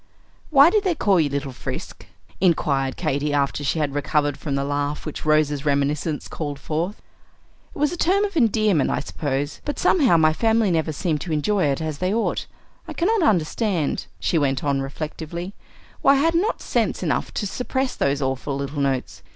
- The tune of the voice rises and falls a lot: Yes, wide, 7.1 semitones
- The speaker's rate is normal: Yes, average, 190 wpm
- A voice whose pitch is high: No, medium, 155 Hz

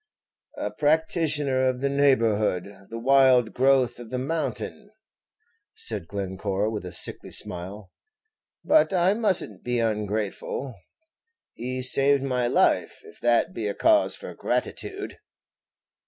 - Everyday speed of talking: No, slow, 125 wpm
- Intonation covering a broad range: No, average, 4.7 semitones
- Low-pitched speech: Yes, low, 125 Hz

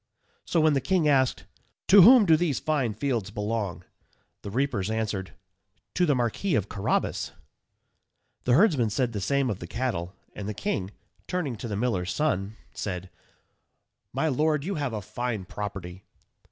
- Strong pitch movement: Yes, wide, 6.6 semitones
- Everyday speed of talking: Yes, average, 160 wpm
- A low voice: Yes, low, 120 Hz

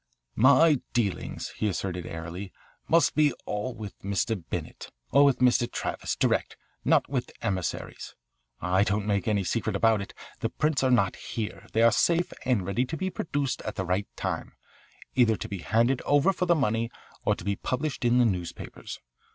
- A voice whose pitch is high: No, low, 115 Hz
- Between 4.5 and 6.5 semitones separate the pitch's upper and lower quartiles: Yes, average, 5.1 semitones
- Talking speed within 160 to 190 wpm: Yes, average, 180 wpm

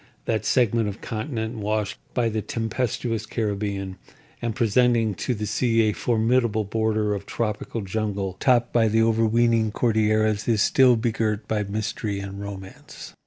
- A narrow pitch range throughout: Yes, narrow, 1.8 semitones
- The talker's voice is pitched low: Yes, low, 110 Hz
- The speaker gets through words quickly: No, average, 145 wpm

